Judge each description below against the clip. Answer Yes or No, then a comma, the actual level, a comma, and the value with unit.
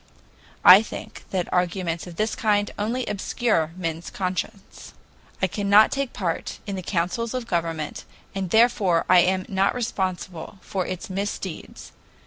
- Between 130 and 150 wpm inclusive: Yes, average, 140 wpm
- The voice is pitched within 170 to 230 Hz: Yes, high, 190 Hz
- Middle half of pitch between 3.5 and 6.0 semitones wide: No, average, 3.0 semitones